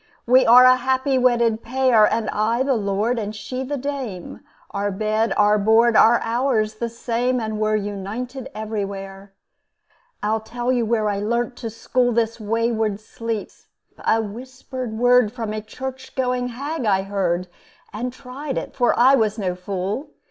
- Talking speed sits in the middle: Yes, average, 165 wpm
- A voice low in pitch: No, high, 230 Hz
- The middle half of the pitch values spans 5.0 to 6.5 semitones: No, average, 3.0 semitones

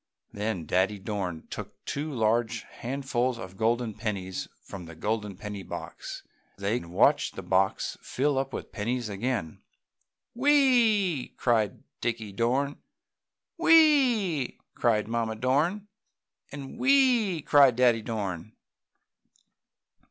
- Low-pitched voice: Yes, low, 120 Hz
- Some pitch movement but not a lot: No, wide, 5.8 semitones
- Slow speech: Yes, slow, 115 wpm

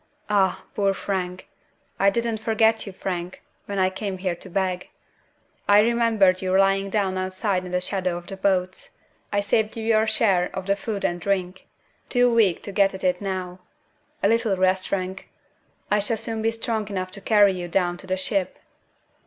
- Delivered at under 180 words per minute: No, average, 185 wpm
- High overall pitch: Yes, high, 195 Hz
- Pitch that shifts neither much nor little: No, narrow, 2.2 semitones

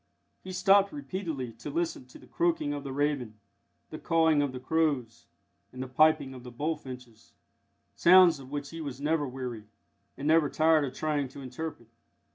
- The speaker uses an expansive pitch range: No, average, 4.0 semitones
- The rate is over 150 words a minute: Yes, average, 175 wpm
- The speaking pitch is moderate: Yes, medium, 145 Hz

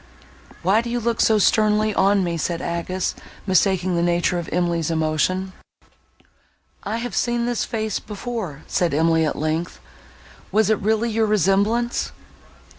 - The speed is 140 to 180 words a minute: Yes, average, 145 wpm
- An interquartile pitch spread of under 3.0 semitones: No, average, 4.3 semitones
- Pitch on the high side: Yes, high, 195 Hz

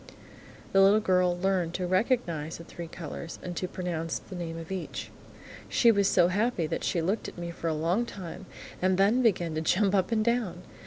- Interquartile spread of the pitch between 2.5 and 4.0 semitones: Yes, average, 2.9 semitones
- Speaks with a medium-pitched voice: Yes, medium, 180 Hz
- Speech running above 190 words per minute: Yes, fast, 205 wpm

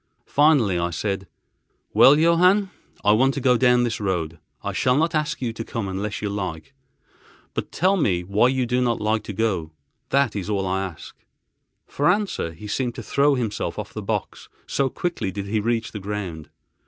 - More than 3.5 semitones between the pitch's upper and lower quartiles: Yes, wide, 5.6 semitones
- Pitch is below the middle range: Yes, low, 110 Hz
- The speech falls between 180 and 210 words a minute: Yes, average, 190 wpm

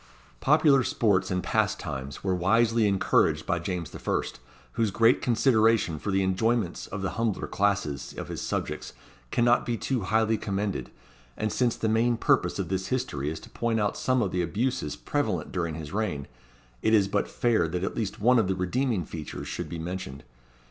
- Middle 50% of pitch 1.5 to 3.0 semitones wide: No, average, 4.1 semitones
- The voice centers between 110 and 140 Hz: No, low, 100 Hz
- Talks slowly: No, average, 185 wpm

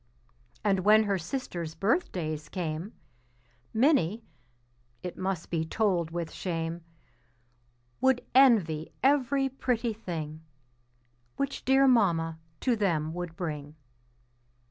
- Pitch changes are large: Yes, wide, 6.4 semitones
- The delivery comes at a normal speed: No, slow, 100 wpm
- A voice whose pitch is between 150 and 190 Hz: Yes, medium, 185 Hz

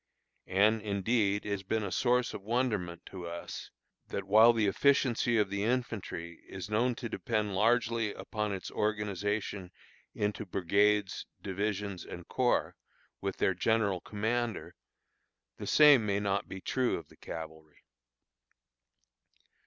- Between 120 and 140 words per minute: Yes, slow, 135 wpm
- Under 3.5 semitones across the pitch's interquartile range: Yes, average, 2.9 semitones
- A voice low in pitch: Yes, low, 105 Hz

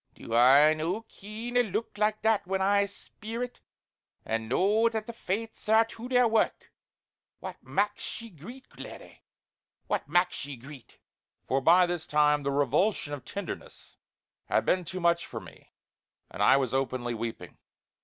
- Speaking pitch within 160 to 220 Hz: Yes, medium, 185 Hz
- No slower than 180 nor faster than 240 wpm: No, average, 165 wpm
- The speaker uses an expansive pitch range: Yes, wide, 7.6 semitones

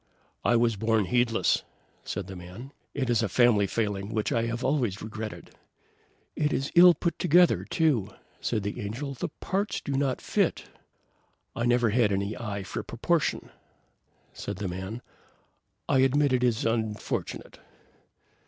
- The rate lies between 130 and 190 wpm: Yes, average, 150 wpm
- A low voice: Yes, low, 115 Hz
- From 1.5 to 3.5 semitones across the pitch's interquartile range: No, average, 4.4 semitones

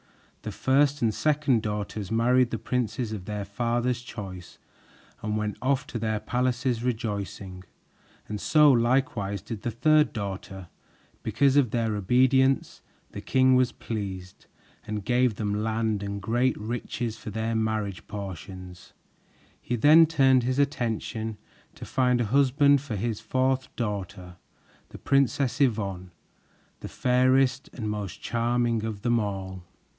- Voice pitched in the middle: No, low, 115 Hz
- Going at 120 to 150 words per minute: Yes, average, 140 wpm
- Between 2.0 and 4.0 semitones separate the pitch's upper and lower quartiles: Yes, average, 3.7 semitones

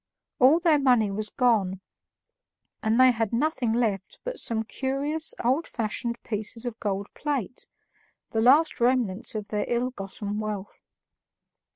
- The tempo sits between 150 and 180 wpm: No, average, 140 wpm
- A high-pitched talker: Yes, high, 235 Hz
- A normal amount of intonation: Yes, average, 3.7 semitones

